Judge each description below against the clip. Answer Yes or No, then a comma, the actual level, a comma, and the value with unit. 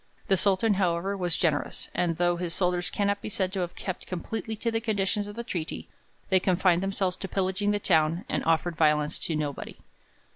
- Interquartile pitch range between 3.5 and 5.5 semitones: No, average, 2.8 semitones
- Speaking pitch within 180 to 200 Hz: Yes, medium, 185 Hz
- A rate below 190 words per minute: No, average, 195 wpm